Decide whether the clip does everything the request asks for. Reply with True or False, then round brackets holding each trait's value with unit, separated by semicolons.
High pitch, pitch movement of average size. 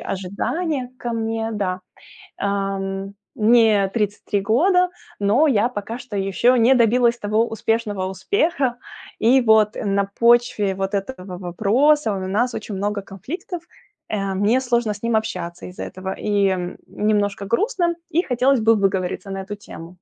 True (215 Hz; 3.6 semitones)